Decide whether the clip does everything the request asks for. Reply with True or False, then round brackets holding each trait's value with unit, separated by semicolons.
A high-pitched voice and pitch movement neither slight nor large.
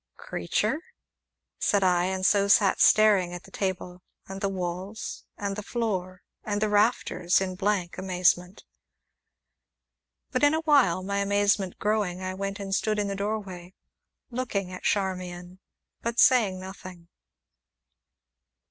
False (195 Hz; 2.3 semitones)